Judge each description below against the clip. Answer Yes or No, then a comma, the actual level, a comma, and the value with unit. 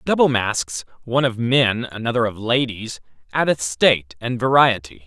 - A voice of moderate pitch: No, low, 115 Hz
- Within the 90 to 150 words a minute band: Yes, average, 140 wpm